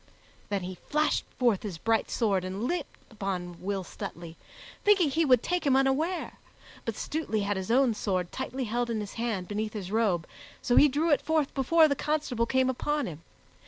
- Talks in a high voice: Yes, high, 235 Hz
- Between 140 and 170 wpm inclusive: No, average, 190 wpm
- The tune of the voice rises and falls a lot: Yes, wide, 6.5 semitones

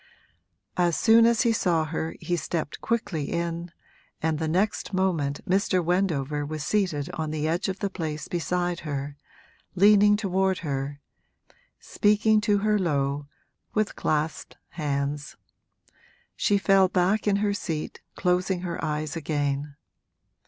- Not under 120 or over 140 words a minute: Yes, slow, 135 wpm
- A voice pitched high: No, medium, 175 Hz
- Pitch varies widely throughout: No, average, 4.5 semitones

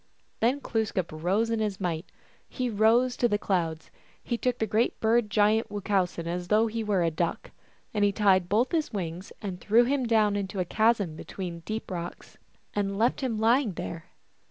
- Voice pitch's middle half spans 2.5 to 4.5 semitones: Yes, average, 3.9 semitones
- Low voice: No, high, 210 Hz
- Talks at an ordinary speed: Yes, average, 180 wpm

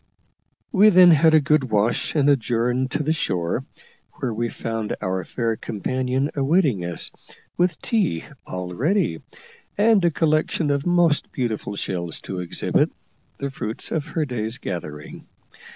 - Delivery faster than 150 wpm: No, average, 145 wpm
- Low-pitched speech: Yes, low, 130 Hz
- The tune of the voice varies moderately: No, wide, 6.8 semitones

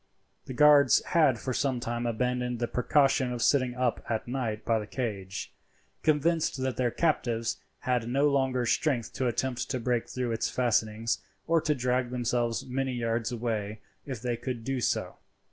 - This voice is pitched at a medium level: No, low, 125 Hz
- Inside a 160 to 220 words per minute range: Yes, average, 170 wpm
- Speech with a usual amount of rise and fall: No, narrow, 2.2 semitones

